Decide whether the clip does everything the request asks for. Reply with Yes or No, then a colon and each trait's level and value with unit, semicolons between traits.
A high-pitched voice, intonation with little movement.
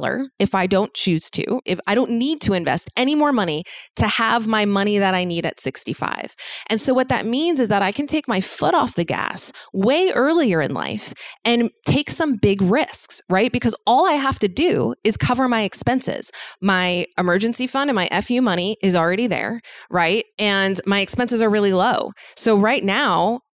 No: high, 220 Hz; average, 4.6 semitones